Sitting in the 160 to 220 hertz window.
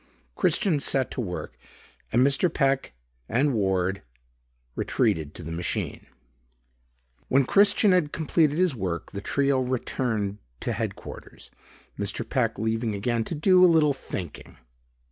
No: low, 130 Hz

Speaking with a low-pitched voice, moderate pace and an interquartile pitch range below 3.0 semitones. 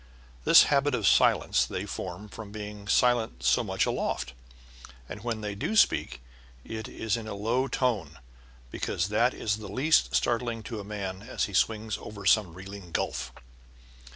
Yes: low, 105 Hz; average, 165 wpm; narrow, 2.5 semitones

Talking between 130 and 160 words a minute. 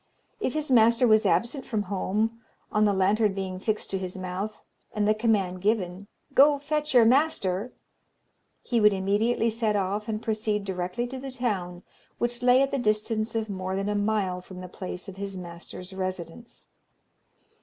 No: average, 175 wpm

